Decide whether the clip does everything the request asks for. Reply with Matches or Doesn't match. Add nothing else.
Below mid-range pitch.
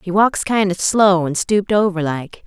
Doesn't match